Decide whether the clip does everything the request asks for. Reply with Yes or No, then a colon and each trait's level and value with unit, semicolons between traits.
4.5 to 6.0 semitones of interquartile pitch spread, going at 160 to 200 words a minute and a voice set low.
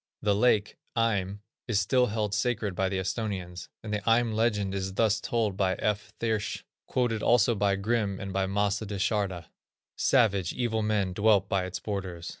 No: narrow, 2.4 semitones; average, 175 wpm; low, 105 Hz